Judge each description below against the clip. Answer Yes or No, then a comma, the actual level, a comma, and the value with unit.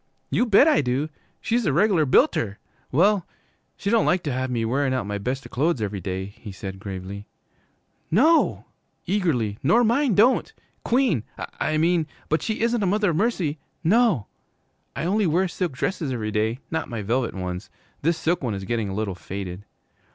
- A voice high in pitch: No, medium, 145 Hz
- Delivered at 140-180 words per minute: Yes, average, 175 wpm